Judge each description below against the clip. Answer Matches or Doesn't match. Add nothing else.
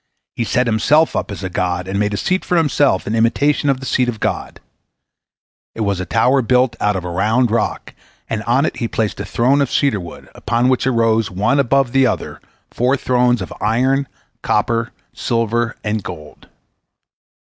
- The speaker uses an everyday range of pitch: Matches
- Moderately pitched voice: Doesn't match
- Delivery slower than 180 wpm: Doesn't match